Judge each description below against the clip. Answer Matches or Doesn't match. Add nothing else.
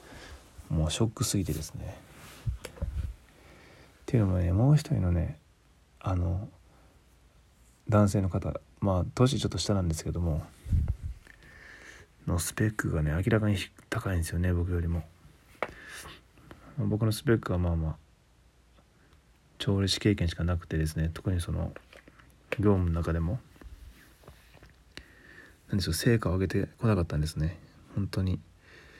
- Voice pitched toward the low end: Matches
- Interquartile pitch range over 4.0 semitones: Matches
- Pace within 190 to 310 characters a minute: Matches